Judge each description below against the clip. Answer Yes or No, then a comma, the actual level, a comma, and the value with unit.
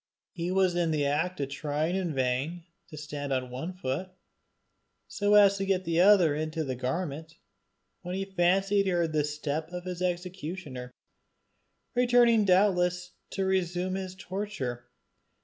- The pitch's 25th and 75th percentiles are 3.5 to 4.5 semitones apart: Yes, average, 4.1 semitones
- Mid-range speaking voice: Yes, medium, 175 Hz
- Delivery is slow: No, average, 150 wpm